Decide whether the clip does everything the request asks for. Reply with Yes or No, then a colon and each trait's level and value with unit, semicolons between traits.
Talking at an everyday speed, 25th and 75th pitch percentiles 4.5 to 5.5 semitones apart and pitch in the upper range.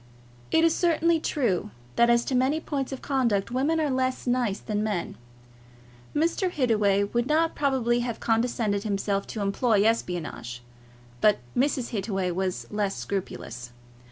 Yes: average, 145 wpm; average, 5.1 semitones; high, 235 Hz